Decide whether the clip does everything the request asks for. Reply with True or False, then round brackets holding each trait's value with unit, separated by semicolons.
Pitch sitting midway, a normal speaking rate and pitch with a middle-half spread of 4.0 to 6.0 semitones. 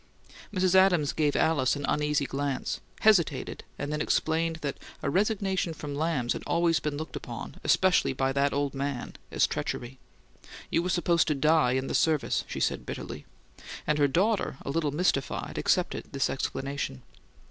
False (150 Hz; 165 wpm; 3.4 semitones)